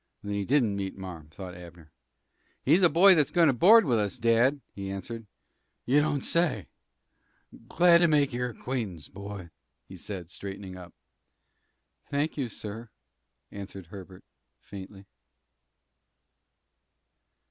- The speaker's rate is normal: No, slow, 130 wpm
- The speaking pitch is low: Yes, low, 105 Hz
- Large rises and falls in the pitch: Yes, wide, 6.9 semitones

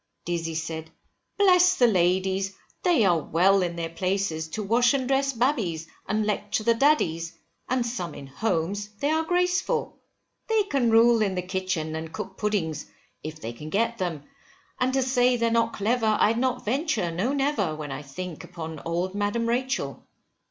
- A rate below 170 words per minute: No, average, 175 wpm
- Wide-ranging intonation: Yes, wide, 6.7 semitones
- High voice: Yes, high, 205 Hz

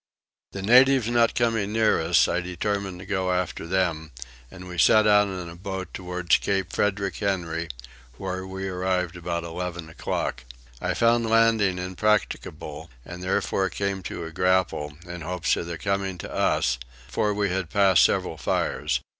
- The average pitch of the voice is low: Yes, very low, 95 Hz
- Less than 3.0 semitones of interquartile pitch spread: Yes, narrow, 2.4 semitones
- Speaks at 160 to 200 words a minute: Yes, average, 165 wpm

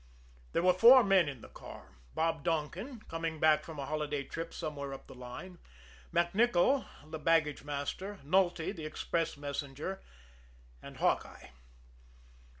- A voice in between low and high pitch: Yes, medium, 160 Hz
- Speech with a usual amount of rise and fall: Yes, average, 4.0 semitones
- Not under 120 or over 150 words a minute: Yes, average, 140 wpm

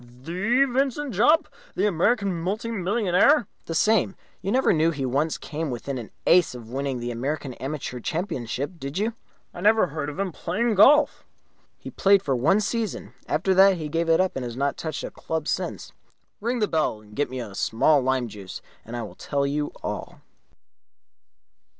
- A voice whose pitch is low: No, medium, 165 Hz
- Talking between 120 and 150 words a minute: No, average, 185 wpm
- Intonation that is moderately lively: No, wide, 7.0 semitones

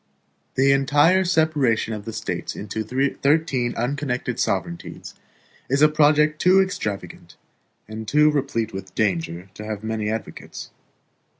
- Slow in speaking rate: Yes, slow, 125 wpm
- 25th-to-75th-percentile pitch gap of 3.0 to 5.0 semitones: No, wide, 5.6 semitones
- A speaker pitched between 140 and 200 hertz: No, low, 130 Hz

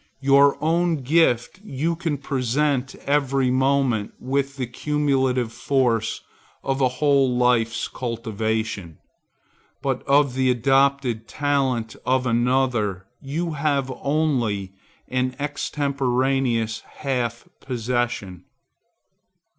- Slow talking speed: Yes, slow, 95 wpm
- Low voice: Yes, low, 130 Hz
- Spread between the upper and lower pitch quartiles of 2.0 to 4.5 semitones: Yes, average, 2.8 semitones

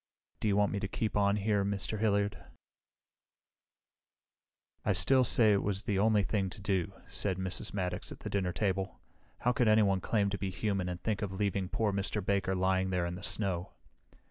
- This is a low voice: Yes, low, 100 Hz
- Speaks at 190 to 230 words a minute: Yes, average, 195 wpm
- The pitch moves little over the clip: Yes, narrow, 1.8 semitones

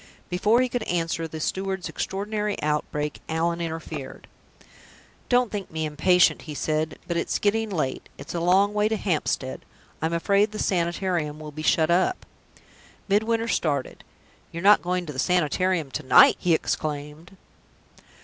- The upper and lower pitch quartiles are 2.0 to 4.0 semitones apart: No, average, 4.4 semitones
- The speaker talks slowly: No, average, 155 wpm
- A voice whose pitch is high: No, medium, 175 Hz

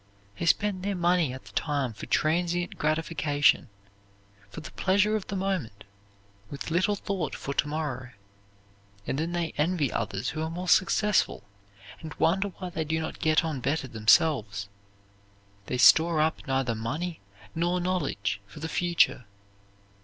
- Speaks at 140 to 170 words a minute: Yes, average, 155 wpm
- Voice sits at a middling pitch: Yes, medium, 160 Hz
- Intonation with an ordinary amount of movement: Yes, average, 4.5 semitones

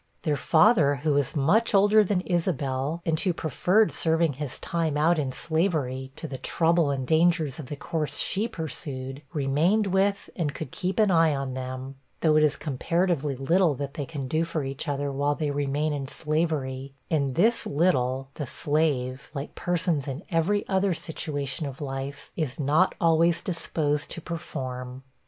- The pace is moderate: Yes, average, 170 wpm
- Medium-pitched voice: Yes, medium, 150 Hz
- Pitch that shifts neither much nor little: Yes, average, 3.7 semitones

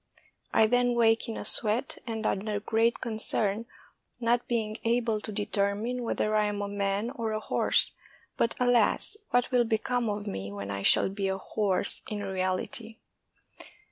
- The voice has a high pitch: Yes, high, 215 Hz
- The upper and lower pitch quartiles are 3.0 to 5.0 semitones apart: No, narrow, 2.5 semitones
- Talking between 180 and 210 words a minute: No, average, 165 wpm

